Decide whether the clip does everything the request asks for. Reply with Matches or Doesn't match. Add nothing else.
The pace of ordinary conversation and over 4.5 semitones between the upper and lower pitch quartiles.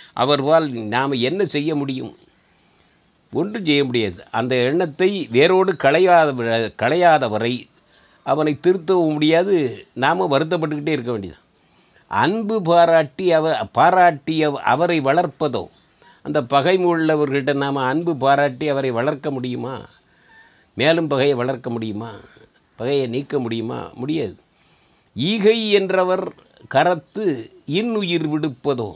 Matches